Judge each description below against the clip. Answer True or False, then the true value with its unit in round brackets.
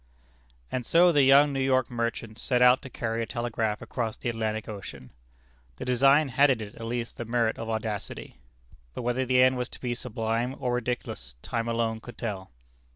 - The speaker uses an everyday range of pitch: False (2.2 semitones)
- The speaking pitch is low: True (120 Hz)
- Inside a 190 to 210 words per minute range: True (195 wpm)